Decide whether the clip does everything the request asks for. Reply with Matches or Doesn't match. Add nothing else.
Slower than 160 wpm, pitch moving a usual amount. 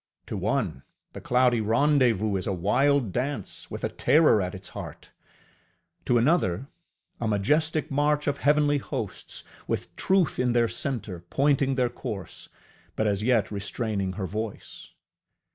Doesn't match